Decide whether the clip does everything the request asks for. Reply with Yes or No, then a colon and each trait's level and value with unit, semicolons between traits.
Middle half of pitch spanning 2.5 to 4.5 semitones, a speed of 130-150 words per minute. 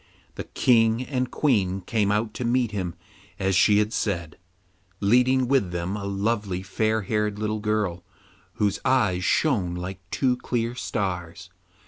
Yes: average, 3.9 semitones; average, 145 wpm